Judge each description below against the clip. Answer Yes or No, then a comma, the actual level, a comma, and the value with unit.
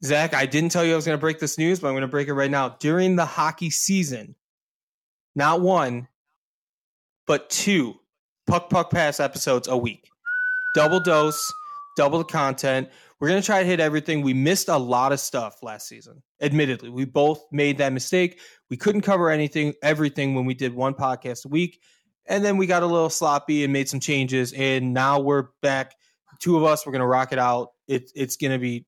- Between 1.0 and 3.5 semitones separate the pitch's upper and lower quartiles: No, average, 4.3 semitones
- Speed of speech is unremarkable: No, fast, 210 wpm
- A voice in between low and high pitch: Yes, medium, 150 Hz